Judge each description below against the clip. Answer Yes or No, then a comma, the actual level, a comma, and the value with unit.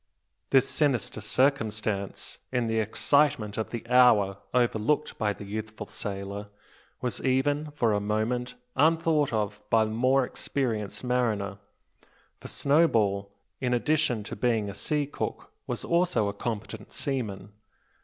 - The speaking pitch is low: Yes, low, 115 Hz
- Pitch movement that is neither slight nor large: Yes, average, 4.5 semitones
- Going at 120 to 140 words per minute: Yes, slow, 135 wpm